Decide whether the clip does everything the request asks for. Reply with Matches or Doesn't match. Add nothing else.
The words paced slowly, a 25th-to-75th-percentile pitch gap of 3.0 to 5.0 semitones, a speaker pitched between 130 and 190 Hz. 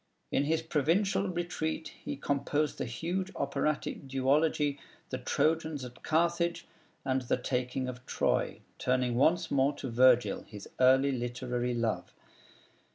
Matches